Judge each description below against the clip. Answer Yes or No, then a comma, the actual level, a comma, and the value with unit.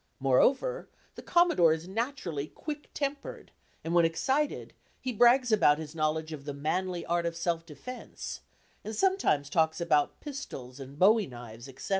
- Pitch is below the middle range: No, medium, 170 Hz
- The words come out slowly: No, average, 155 wpm